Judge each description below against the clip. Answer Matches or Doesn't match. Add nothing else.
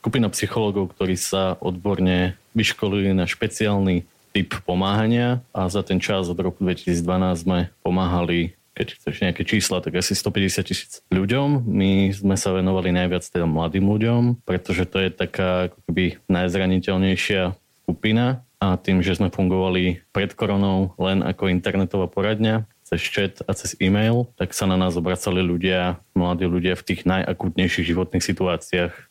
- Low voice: Matches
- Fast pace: Doesn't match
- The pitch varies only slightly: Matches